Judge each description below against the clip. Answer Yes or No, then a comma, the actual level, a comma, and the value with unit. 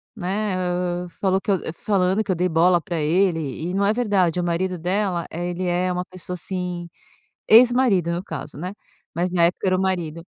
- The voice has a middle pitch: Yes, medium, 180 Hz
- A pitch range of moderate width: No, narrow, 1.7 semitones